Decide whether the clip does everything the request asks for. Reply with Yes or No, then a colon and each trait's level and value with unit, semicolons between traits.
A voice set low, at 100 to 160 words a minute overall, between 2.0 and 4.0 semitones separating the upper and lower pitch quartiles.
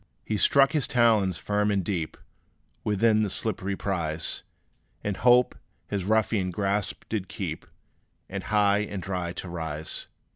Yes: low, 100 Hz; average, 140 wpm; average, 2.7 semitones